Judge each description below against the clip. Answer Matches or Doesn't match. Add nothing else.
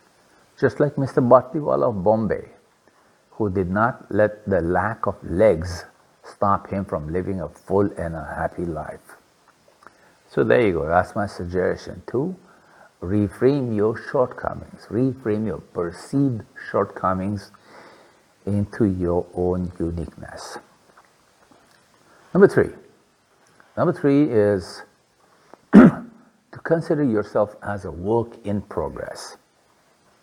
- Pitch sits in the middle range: Doesn't match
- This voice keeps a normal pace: Doesn't match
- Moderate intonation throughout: Matches